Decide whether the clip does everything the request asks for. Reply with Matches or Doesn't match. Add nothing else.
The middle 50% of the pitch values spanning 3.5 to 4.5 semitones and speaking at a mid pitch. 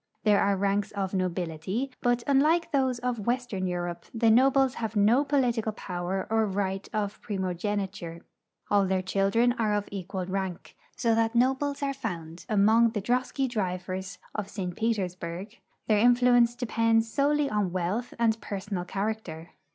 Doesn't match